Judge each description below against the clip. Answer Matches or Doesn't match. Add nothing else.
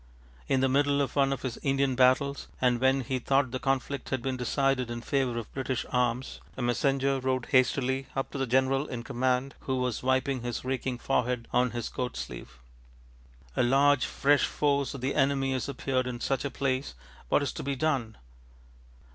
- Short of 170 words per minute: Doesn't match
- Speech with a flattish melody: Matches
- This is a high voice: Doesn't match